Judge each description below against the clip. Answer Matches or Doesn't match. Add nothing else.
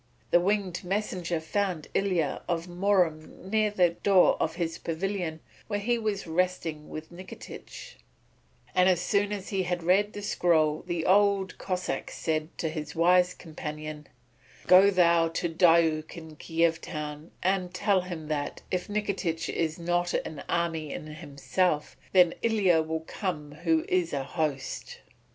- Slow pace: Doesn't match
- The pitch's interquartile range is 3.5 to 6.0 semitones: Doesn't match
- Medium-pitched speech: Matches